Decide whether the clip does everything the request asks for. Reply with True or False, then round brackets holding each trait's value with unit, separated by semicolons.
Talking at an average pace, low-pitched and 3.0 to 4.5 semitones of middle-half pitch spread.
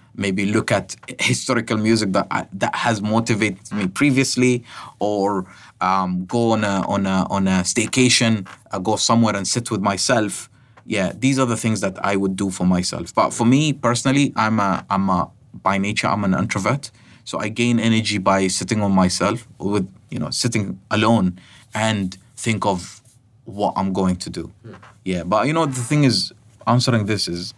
True (180 wpm; 110 Hz; 3.6 semitones)